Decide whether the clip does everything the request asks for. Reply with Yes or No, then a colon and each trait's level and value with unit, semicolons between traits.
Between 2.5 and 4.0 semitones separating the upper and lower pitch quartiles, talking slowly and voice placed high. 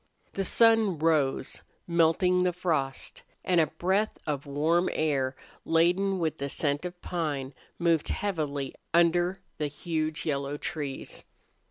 No: average, 3.6 semitones; slow, 130 wpm; medium, 165 Hz